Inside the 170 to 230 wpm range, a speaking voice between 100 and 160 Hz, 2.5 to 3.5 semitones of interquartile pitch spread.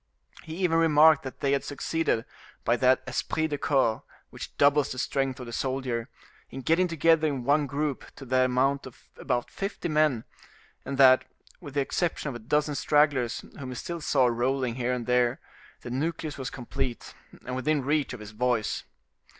Yes: average, 185 wpm; low, 135 Hz; average, 3.1 semitones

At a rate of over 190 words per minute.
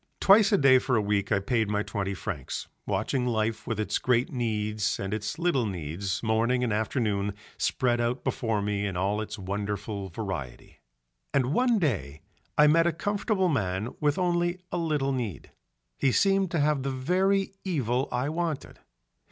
No: average, 170 wpm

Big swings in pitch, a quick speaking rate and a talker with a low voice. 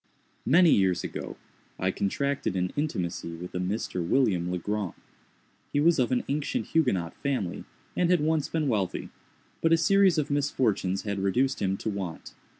No: wide, 8.0 semitones; average, 165 wpm; low, 110 Hz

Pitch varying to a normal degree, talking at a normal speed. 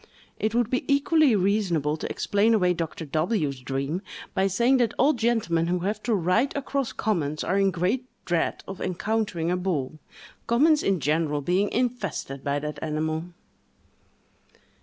No: wide, 6.3 semitones; average, 150 wpm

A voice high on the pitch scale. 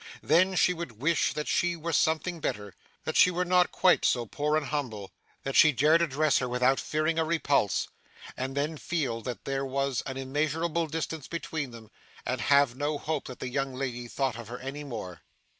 No: medium, 140 Hz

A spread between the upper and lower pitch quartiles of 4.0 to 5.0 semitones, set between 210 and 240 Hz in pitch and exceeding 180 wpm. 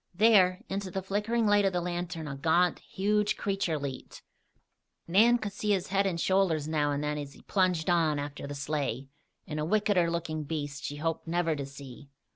No: average, 4.6 semitones; medium, 170 Hz; average, 195 wpm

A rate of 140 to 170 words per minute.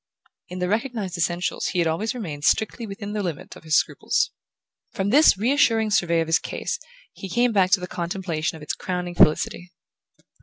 No: average, 185 wpm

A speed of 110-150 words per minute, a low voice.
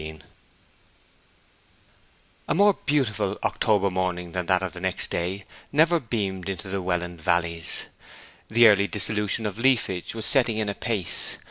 Yes: average, 140 wpm; low, 100 Hz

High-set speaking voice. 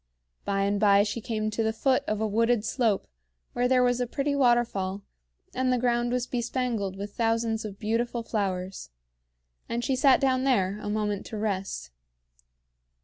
Yes: high, 225 Hz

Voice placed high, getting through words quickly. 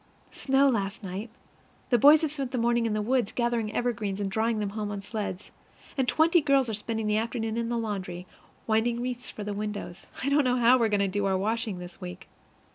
Yes: high, 225 Hz; fast, 225 wpm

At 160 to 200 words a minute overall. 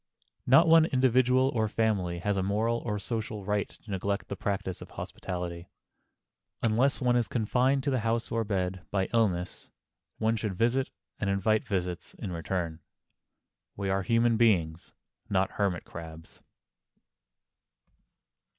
No: average, 145 wpm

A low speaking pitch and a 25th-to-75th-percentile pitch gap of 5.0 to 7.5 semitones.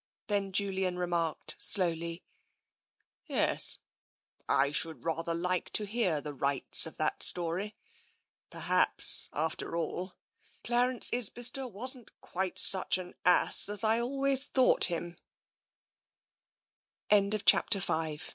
No: high, 190 Hz; wide, 5.6 semitones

